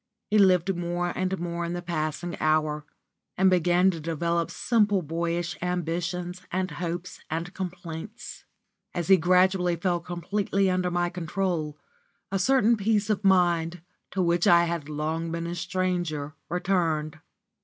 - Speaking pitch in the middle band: Yes, medium, 175 Hz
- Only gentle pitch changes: Yes, narrow, 1.8 semitones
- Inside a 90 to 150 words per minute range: Yes, average, 145 wpm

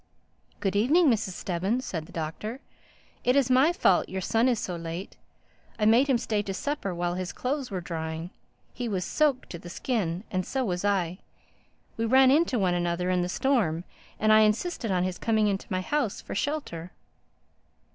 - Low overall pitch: No, high, 205 Hz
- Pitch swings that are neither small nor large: No, wide, 6.0 semitones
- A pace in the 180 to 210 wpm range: Yes, average, 185 wpm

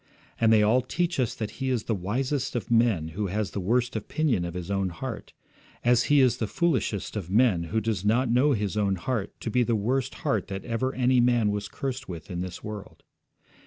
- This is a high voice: No, low, 110 Hz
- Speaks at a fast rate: Yes, fast, 220 wpm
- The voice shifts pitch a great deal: No, average, 4.1 semitones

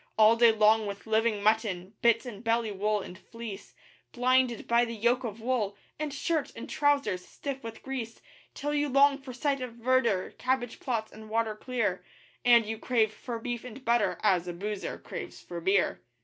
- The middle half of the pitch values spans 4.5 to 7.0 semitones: No, average, 3.0 semitones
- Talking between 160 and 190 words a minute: Yes, average, 185 wpm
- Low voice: No, high, 230 Hz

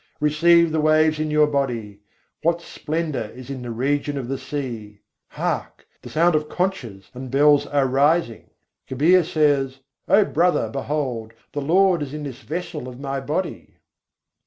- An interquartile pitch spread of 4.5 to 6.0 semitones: No, average, 3.2 semitones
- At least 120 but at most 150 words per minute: No, average, 160 wpm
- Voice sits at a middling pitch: Yes, medium, 145 Hz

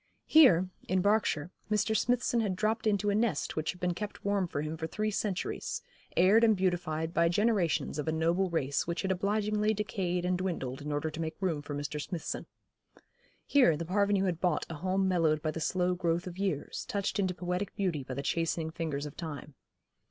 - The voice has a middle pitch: Yes, medium, 180 Hz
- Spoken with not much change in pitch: No, average, 4.0 semitones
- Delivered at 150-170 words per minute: No, average, 200 wpm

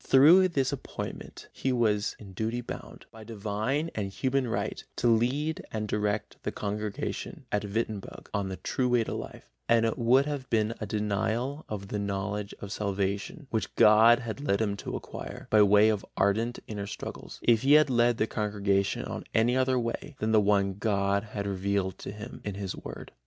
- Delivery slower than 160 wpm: No, average, 190 wpm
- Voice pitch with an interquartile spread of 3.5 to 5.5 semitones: No, average, 3.1 semitones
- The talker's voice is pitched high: No, low, 110 Hz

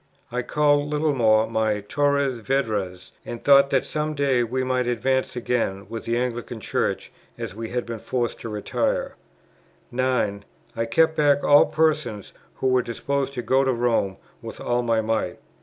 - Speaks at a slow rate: No, average, 165 wpm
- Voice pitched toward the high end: No, low, 125 Hz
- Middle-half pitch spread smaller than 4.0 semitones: Yes, average, 3.5 semitones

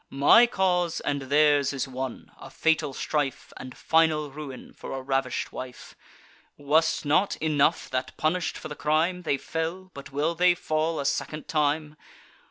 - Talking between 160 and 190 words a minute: Yes, average, 165 wpm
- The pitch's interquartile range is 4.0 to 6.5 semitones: No, narrow, 2.6 semitones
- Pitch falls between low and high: Yes, medium, 150 Hz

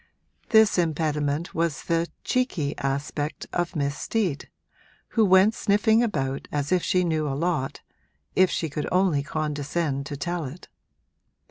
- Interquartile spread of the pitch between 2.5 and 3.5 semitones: No, average, 4.1 semitones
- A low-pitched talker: No, medium, 160 Hz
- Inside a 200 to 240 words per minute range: No, average, 140 wpm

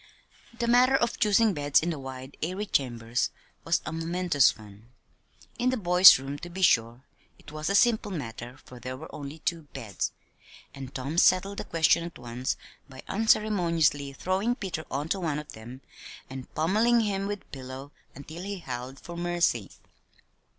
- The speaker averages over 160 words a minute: Yes, average, 170 wpm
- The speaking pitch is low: No, medium, 160 Hz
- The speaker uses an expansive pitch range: Yes, wide, 6.5 semitones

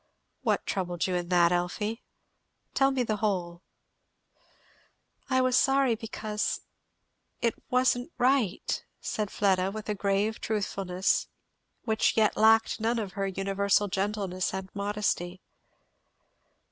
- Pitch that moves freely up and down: No, average, 2.9 semitones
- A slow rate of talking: Yes, slow, 120 wpm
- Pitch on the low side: No, high, 205 Hz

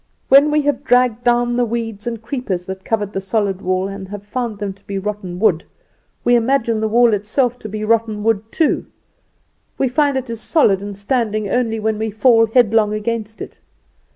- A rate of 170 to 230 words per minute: Yes, average, 195 wpm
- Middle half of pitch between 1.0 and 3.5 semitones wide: Yes, average, 2.9 semitones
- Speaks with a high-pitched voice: Yes, high, 220 Hz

